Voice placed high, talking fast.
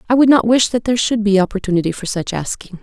Yes: high, 210 Hz; fast, 255 wpm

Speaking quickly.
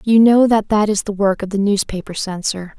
Yes: fast, 235 wpm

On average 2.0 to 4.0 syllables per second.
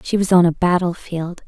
No: 5.2 syllables/s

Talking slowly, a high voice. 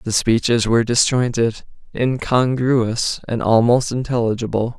No: slow, 90 wpm; low, 120 Hz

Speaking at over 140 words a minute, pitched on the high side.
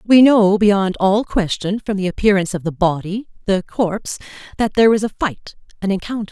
Yes: average, 170 wpm; high, 200 Hz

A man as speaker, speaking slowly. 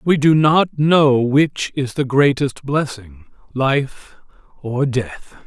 Yes: male; slow, 130 wpm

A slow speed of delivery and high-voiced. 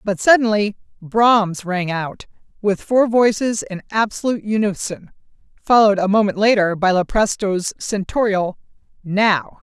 Yes: slow, 115 wpm; high, 205 Hz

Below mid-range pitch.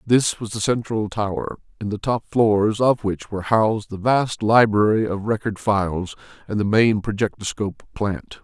Yes: low, 105 Hz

